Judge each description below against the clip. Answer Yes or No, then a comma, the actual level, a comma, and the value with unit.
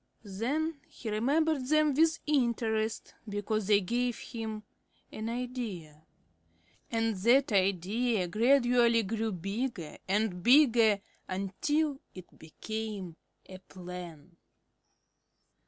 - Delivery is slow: Yes, slow, 95 wpm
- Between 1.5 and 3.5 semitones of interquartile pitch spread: No, average, 4.6 semitones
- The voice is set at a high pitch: Yes, high, 220 Hz